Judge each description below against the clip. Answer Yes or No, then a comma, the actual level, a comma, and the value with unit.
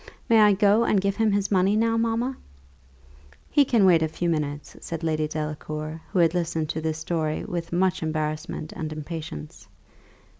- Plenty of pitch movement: No, average, 4.6 semitones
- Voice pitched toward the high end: No, medium, 165 Hz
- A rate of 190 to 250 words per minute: No, average, 175 wpm